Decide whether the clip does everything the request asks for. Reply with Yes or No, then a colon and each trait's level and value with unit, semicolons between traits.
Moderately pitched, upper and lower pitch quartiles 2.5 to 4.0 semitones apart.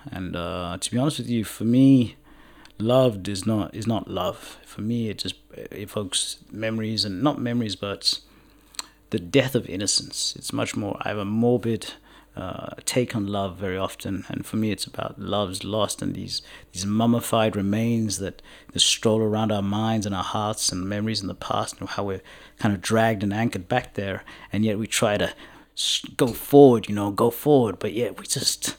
No: low, 110 Hz; average, 2.8 semitones